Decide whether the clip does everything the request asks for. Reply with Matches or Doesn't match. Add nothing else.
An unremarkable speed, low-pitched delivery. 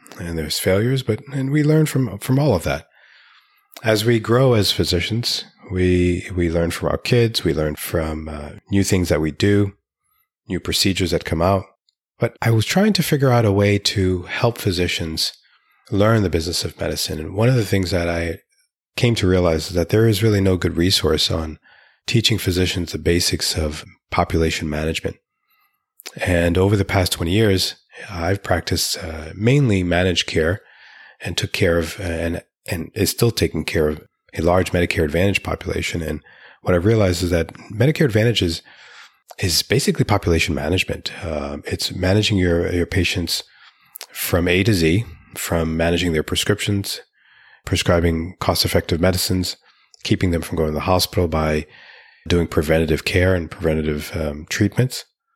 Matches